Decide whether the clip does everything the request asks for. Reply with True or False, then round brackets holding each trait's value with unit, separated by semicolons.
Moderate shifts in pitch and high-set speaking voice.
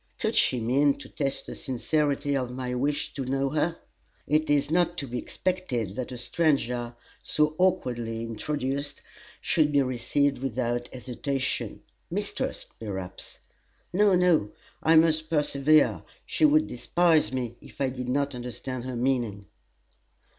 False (3.7 semitones; 135 Hz)